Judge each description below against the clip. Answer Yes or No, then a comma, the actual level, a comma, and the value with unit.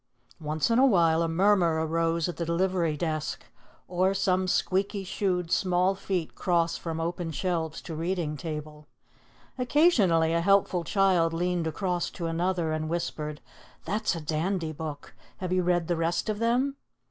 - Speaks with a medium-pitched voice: Yes, medium, 175 Hz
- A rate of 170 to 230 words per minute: No, average, 160 wpm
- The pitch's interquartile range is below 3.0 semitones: Yes, narrow, 2.5 semitones